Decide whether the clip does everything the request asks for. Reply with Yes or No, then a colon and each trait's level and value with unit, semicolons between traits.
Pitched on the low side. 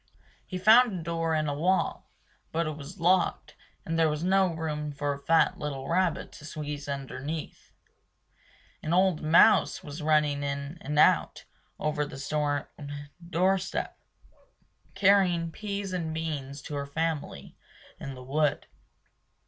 No: medium, 155 Hz